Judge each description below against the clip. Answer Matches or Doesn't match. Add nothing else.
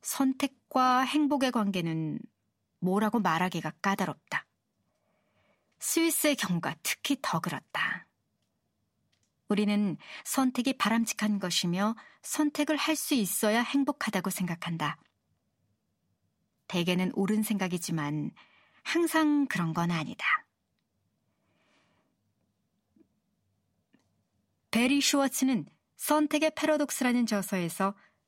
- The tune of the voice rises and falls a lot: Matches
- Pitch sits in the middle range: Doesn't match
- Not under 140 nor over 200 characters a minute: Doesn't match